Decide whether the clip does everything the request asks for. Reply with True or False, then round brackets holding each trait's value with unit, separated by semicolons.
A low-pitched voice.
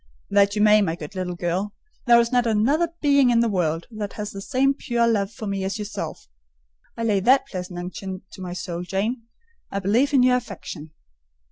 False (205 Hz)